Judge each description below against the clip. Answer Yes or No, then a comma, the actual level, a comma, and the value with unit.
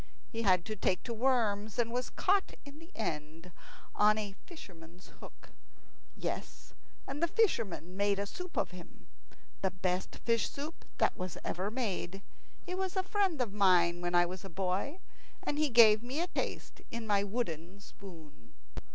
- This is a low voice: No, high, 205 Hz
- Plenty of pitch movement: Yes, wide, 6.0 semitones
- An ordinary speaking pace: Yes, average, 170 wpm